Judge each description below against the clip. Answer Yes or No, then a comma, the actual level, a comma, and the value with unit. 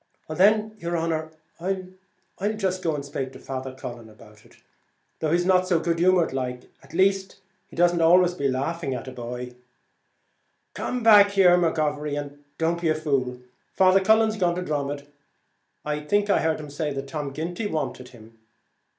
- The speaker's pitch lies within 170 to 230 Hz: No, medium, 160 Hz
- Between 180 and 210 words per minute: No, average, 165 wpm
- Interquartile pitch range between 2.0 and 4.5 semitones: No, average, 5.0 semitones